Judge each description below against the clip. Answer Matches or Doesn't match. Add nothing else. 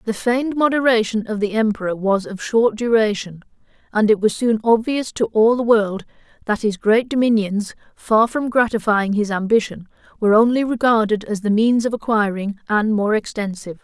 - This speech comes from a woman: Matches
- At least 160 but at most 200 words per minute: Matches